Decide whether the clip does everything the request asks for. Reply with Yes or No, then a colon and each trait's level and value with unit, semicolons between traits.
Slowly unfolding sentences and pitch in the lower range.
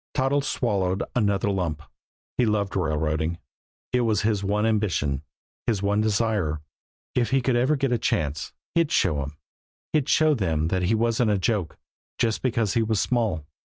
No: average, 165 wpm; low, 105 Hz